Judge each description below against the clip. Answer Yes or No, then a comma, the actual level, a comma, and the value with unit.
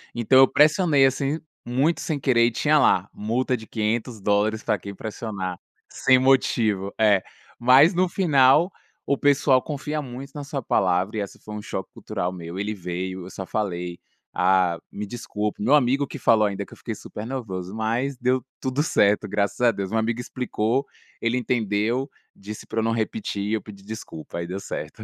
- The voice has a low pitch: Yes, low, 110 Hz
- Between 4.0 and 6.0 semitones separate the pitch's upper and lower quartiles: Yes, average, 4.7 semitones